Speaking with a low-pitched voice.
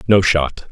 Yes: very low, 90 Hz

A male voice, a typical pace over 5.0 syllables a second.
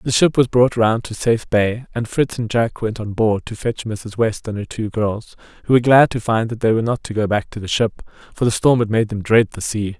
Yes: male; 5.5 syllables/s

